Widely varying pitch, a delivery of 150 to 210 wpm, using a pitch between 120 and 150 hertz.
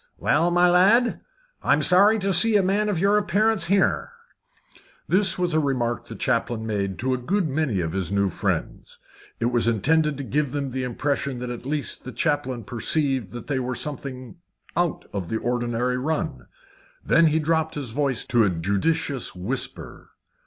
Yes: wide, 5.7 semitones; average, 175 wpm; medium, 140 Hz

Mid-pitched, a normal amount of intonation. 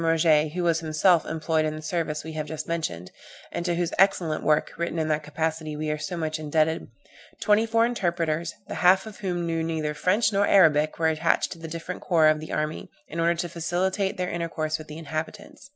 No: medium, 165 Hz; narrow, 2.1 semitones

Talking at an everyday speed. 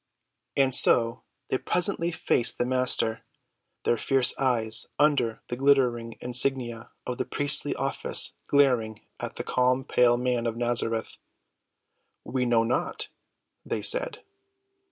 No: slow, 125 wpm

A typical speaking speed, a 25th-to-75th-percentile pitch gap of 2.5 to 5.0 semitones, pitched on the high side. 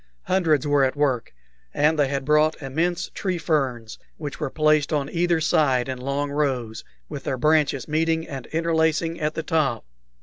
No: average, 170 wpm; average, 2.9 semitones; medium, 150 Hz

